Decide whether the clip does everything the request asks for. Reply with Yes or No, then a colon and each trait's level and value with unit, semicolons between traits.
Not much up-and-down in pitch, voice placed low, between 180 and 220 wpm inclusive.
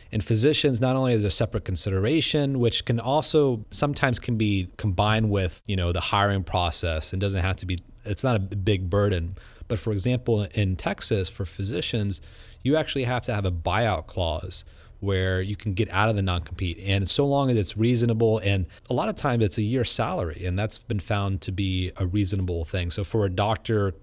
No: average, 3.7 semitones; low, 105 Hz; fast, 205 wpm